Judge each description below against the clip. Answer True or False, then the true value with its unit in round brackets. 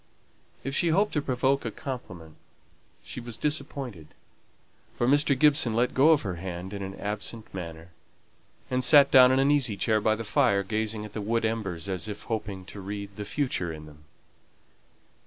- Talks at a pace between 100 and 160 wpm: False (175 wpm)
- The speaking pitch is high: False (110 Hz)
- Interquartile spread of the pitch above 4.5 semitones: True (5.4 semitones)